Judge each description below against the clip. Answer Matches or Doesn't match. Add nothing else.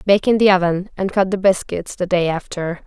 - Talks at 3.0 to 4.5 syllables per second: Doesn't match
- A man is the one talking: Doesn't match